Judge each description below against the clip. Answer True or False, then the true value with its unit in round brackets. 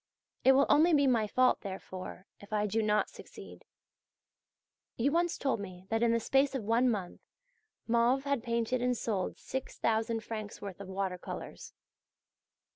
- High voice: True (230 Hz)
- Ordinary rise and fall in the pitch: True (3.9 semitones)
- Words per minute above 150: True (160 wpm)